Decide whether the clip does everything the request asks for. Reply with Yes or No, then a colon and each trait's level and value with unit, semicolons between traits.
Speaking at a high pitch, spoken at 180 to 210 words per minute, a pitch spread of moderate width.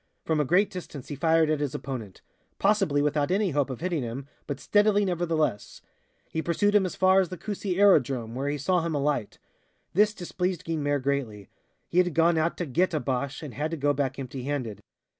No: medium, 155 Hz; fast, 205 wpm; average, 4.6 semitones